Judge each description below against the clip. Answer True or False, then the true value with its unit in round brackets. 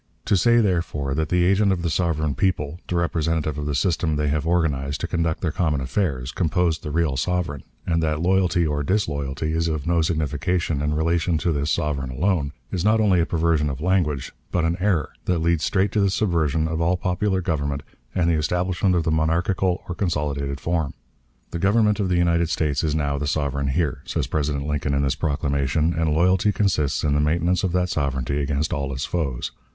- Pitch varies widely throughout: False (3.4 semitones)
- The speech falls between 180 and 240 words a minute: True (200 wpm)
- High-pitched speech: False (80 Hz)